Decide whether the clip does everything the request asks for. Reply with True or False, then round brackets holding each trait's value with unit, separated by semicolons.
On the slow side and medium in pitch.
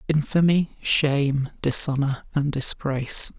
True (90 wpm; 145 Hz)